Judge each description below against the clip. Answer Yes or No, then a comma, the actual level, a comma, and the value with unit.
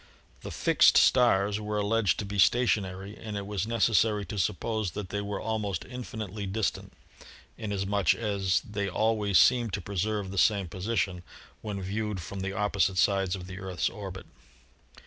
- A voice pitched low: Yes, low, 100 Hz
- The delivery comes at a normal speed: Yes, average, 165 wpm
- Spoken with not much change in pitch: Yes, narrow, 2.0 semitones